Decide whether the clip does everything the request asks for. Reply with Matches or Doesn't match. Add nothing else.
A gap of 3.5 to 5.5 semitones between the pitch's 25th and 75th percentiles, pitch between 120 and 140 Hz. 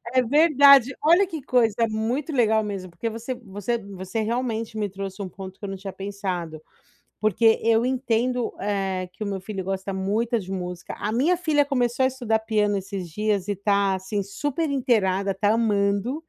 Doesn't match